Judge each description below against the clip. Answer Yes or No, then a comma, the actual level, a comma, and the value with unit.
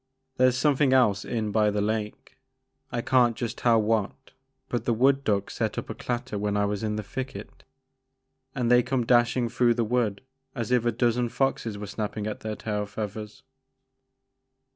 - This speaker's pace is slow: No, average, 185 wpm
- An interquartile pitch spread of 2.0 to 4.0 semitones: Yes, average, 2.7 semitones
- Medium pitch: No, low, 115 Hz